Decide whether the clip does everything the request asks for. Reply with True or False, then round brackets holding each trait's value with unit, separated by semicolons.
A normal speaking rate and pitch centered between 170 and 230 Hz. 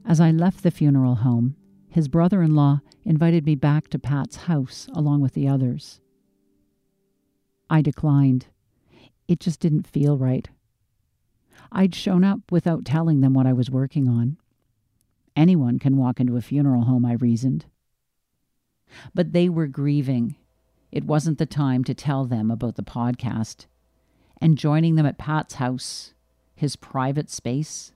False (150 wpm; 140 Hz)